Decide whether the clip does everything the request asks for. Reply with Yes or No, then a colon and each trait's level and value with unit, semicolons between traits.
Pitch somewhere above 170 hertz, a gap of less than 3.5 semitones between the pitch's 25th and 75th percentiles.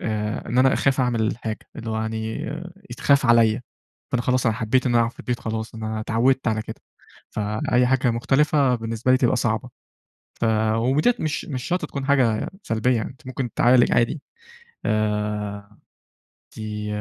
No: low, 115 Hz; average, 2.7 semitones